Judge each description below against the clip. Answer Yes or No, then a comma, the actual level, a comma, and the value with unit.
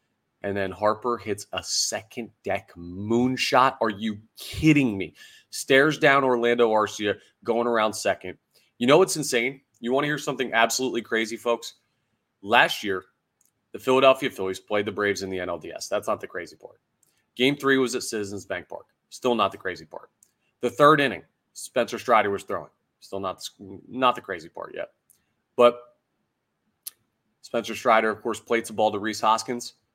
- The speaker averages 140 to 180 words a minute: Yes, average, 170 wpm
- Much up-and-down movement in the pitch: No, average, 3.5 semitones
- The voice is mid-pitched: No, low, 115 Hz